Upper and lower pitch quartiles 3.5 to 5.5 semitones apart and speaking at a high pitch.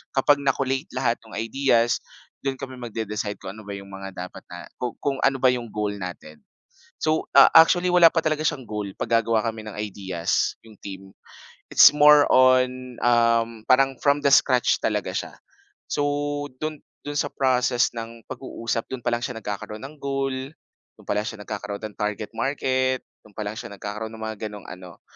No: average, 4.2 semitones; low, 120 Hz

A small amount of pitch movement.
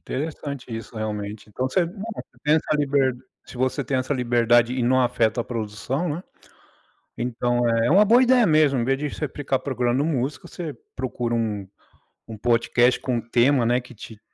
No: average, 3.4 semitones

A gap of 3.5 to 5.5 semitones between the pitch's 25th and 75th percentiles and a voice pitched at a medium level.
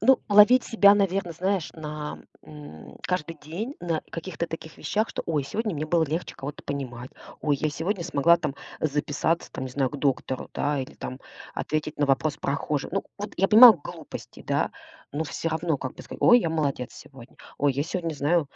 Yes: average, 3.8 semitones; medium, 155 Hz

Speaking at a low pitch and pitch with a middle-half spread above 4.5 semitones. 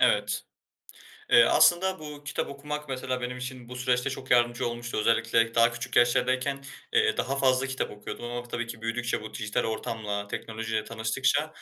No: low, 120 Hz; average, 2.8 semitones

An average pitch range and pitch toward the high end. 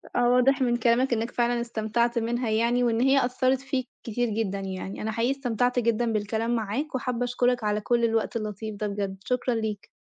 No: narrow, 2.2 semitones; high, 235 Hz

